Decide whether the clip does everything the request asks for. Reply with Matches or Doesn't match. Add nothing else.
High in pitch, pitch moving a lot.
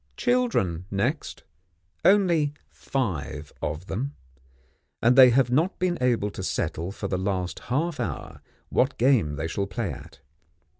Doesn't match